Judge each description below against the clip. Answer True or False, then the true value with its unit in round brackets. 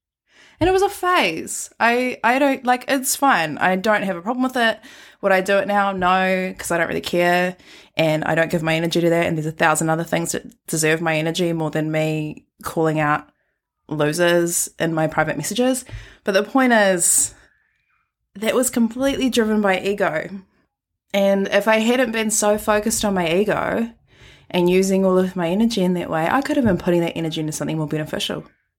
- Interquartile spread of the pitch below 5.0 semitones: False (5.5 semitones)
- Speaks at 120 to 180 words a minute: False (200 wpm)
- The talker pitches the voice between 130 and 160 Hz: False (190 Hz)